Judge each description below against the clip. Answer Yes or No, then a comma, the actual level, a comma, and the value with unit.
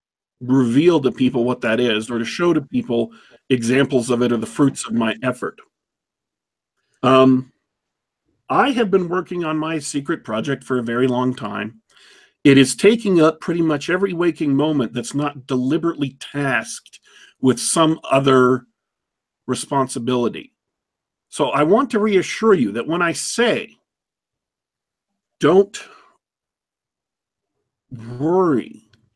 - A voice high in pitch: No, low, 135 Hz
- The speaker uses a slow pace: Yes, slow, 130 wpm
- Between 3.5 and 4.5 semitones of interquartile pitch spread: No, average, 5.0 semitones